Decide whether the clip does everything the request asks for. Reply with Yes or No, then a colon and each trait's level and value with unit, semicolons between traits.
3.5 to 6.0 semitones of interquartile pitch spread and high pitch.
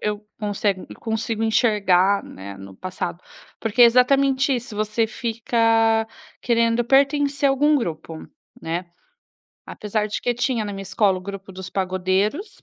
Yes: average, 3.9 semitones; high, 220 Hz